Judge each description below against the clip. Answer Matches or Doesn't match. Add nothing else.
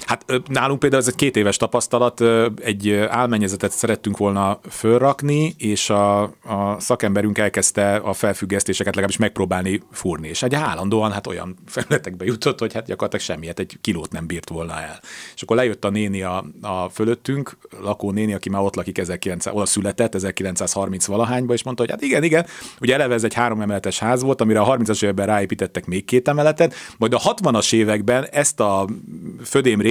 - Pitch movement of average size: Matches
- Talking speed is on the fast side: Matches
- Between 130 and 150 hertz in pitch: Doesn't match